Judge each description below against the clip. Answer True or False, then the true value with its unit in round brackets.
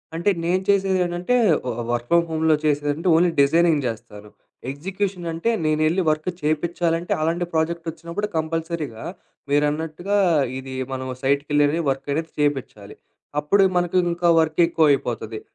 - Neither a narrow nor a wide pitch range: True (3.0 semitones)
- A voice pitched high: False (160 Hz)